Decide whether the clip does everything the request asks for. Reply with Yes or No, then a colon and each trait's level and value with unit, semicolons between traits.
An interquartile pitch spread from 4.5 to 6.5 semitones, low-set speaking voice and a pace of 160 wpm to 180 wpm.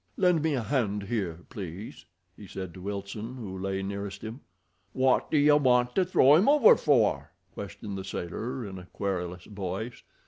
Yes: average, 5.2 semitones; low, 105 Hz; average, 175 wpm